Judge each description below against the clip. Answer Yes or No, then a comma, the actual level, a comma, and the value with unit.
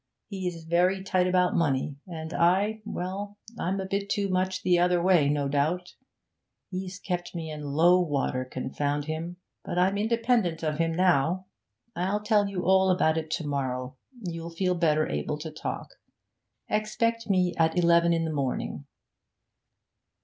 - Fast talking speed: No, average, 155 wpm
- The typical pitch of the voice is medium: Yes, medium, 175 Hz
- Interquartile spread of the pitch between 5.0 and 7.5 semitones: No, average, 3.2 semitones